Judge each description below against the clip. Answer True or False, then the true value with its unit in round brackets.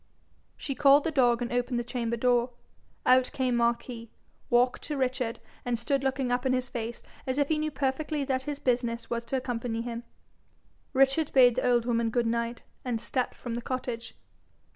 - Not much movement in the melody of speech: True (2.0 semitones)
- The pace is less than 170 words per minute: False (185 wpm)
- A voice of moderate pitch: False (245 Hz)